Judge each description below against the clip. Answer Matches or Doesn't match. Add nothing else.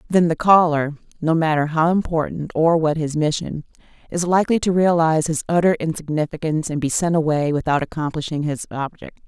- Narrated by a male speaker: Doesn't match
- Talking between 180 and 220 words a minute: Doesn't match